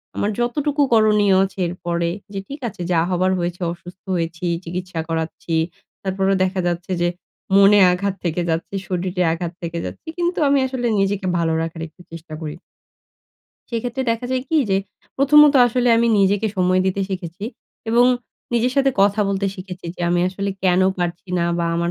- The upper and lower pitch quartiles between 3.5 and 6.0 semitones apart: Yes, average, 4.1 semitones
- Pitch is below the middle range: No, high, 190 Hz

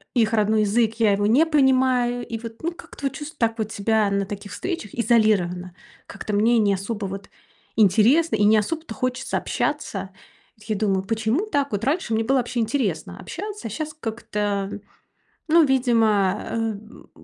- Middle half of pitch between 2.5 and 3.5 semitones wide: No, average, 4.0 semitones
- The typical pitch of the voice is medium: No, high, 225 Hz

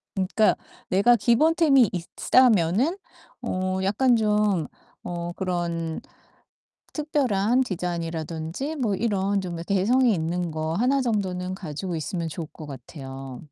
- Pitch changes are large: Yes, wide, 5.7 semitones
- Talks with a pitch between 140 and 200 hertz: Yes, medium, 185 Hz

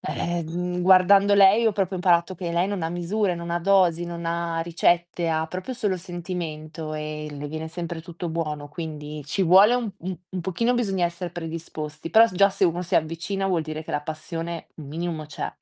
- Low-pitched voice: No, medium, 170 Hz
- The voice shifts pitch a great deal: No, narrow, 2.5 semitones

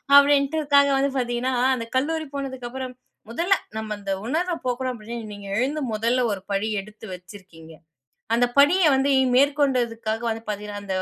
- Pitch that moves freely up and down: No, average, 4.7 semitones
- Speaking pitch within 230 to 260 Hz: Yes, high, 245 Hz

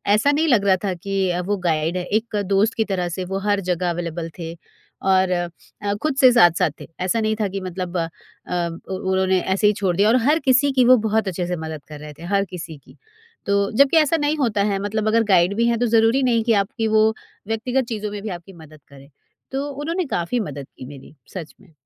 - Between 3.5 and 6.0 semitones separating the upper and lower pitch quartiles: Yes, average, 4.7 semitones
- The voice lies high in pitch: Yes, high, 200 Hz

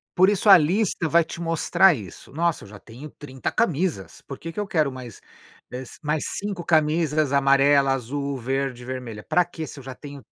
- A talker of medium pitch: Yes, medium, 145 Hz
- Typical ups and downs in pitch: Yes, average, 4.3 semitones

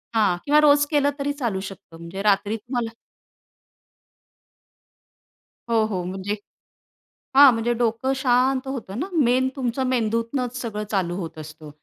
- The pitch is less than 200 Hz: No, high, 230 Hz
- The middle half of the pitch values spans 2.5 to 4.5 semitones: No, average, 5.0 semitones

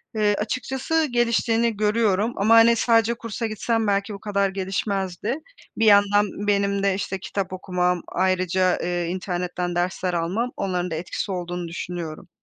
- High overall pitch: Yes, high, 200 Hz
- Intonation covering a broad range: No, average, 3.3 semitones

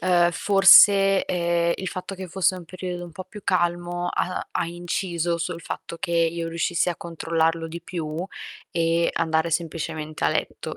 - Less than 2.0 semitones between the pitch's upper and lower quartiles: Yes, narrow, 1.6 semitones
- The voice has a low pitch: No, medium, 170 Hz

